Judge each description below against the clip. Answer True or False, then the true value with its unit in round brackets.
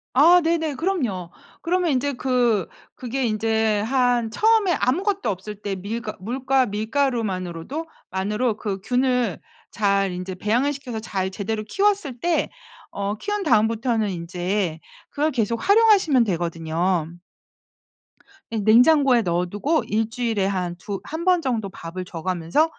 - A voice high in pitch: True (225 Hz)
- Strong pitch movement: True (6.0 semitones)